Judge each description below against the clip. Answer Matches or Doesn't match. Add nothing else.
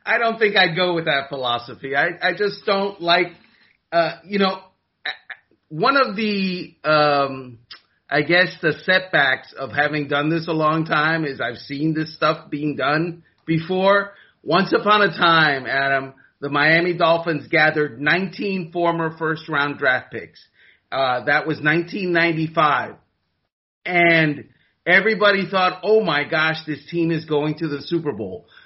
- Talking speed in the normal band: Matches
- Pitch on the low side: Doesn't match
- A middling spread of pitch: Matches